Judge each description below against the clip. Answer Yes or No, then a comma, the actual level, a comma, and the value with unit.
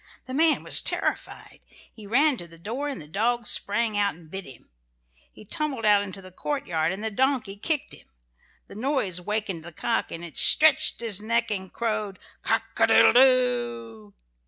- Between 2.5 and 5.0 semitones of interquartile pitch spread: No, wide, 5.5 semitones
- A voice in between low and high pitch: No, high, 210 Hz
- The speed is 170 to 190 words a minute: Yes, average, 180 wpm